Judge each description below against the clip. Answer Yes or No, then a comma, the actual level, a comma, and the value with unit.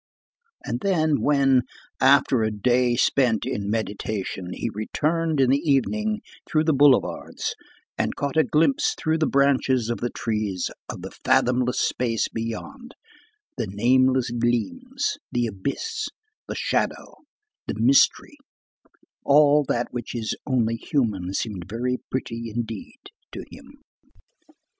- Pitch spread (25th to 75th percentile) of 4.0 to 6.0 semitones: Yes, average, 4.6 semitones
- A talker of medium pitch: No, low, 125 Hz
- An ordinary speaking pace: No, slow, 130 wpm